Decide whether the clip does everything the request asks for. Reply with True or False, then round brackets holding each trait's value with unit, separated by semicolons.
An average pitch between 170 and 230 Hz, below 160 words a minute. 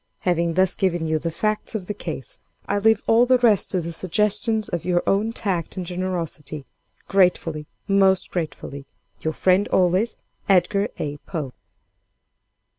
True (185 Hz; 150 wpm)